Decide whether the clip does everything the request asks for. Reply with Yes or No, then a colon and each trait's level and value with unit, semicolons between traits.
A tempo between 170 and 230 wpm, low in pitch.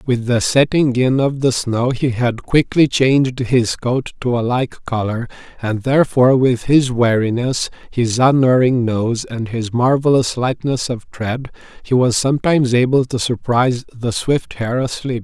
No: average, 160 wpm; low, 125 Hz